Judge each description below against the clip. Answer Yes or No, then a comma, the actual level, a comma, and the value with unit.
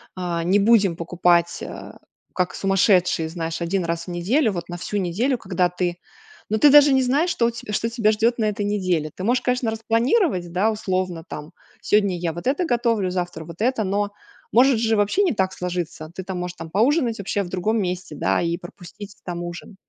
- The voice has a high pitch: Yes, high, 195 Hz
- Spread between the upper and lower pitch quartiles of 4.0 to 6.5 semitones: Yes, average, 4.5 semitones